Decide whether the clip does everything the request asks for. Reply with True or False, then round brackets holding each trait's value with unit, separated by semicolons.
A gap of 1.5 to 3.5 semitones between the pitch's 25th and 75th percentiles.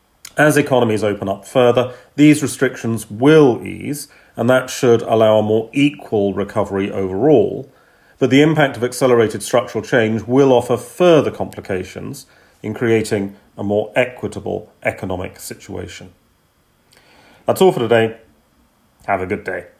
False (4.1 semitones)